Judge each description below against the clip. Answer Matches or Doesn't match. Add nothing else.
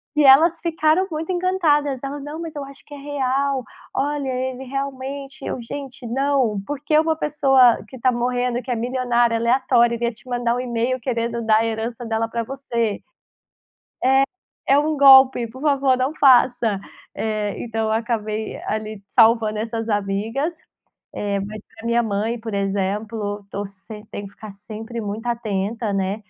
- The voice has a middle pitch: Doesn't match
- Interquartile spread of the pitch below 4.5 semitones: Matches